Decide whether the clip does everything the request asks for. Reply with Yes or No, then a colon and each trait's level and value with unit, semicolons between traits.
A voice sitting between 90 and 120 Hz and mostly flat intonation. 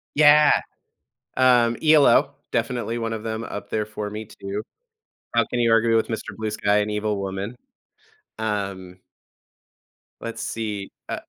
Yes: low, 110 Hz; narrow, 2.1 semitones